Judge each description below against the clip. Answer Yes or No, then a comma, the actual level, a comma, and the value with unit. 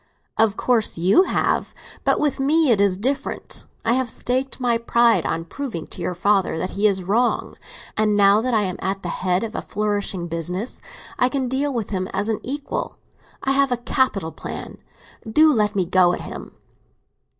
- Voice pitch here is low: No, high, 215 Hz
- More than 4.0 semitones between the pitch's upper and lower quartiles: Yes, average, 5.0 semitones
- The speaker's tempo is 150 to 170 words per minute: No, average, 185 wpm